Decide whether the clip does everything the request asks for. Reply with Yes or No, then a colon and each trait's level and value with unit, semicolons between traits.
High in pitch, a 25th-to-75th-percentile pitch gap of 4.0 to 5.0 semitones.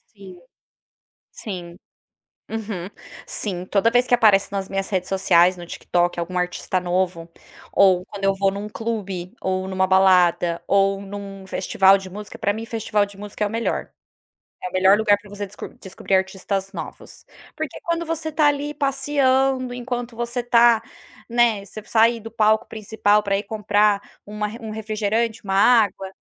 No: high, 205 Hz; average, 3.1 semitones